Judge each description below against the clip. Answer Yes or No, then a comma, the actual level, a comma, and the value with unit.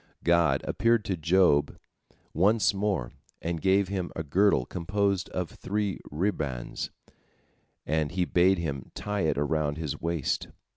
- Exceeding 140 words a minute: No, slow, 135 wpm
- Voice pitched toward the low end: Yes, very low, 85 Hz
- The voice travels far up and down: No, average, 4.2 semitones